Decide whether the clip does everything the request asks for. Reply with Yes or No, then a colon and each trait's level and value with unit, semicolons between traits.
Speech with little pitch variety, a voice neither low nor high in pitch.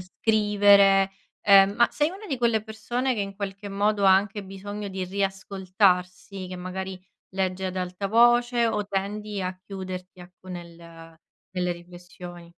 No: narrow, 2.2 semitones; high, 195 Hz